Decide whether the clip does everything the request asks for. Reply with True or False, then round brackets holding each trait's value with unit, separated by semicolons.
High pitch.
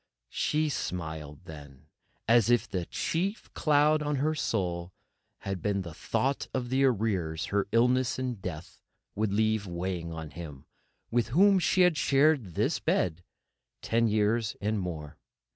False (105 Hz)